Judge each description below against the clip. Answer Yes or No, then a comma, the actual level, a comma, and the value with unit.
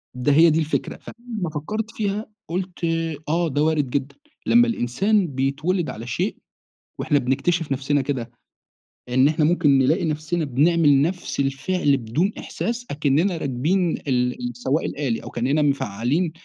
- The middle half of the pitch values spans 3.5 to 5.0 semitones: Yes, average, 4.6 semitones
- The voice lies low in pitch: No, medium, 150 Hz